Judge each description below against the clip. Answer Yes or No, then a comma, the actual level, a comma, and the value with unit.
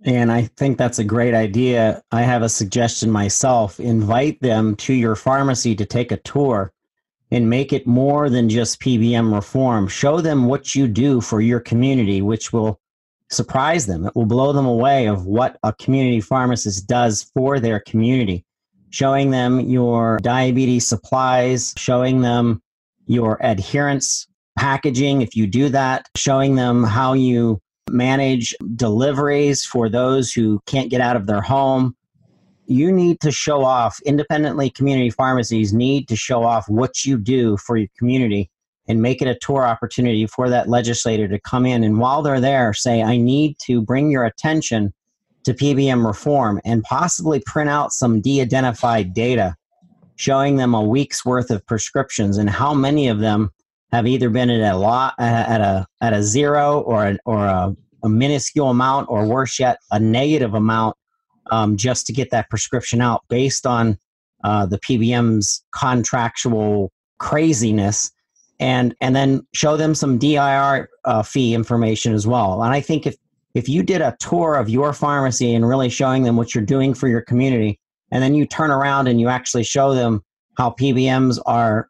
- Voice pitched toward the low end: Yes, low, 125 Hz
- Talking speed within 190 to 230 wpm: No, average, 170 wpm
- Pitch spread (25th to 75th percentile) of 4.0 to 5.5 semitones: No, average, 3.2 semitones